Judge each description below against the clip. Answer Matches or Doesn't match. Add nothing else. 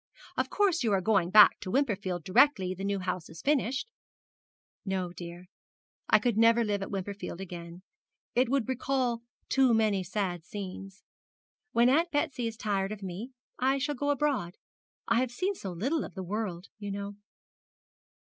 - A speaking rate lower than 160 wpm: Doesn't match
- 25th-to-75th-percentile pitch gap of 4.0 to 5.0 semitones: Doesn't match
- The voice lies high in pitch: Matches